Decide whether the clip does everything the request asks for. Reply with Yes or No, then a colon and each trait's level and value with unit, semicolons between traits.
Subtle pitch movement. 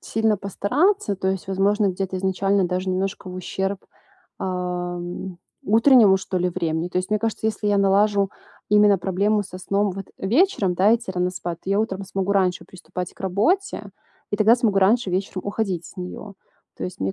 Yes: narrow, 2.2 semitones